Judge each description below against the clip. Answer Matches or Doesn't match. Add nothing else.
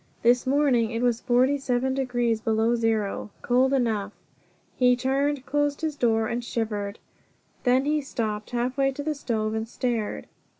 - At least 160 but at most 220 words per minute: Doesn't match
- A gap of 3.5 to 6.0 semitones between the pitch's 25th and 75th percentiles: Doesn't match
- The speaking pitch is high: Matches